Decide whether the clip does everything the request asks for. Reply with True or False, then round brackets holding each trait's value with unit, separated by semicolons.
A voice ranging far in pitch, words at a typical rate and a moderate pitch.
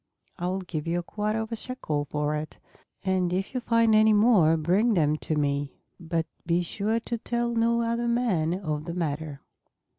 True (6.3 semitones; 190 wpm; 180 Hz)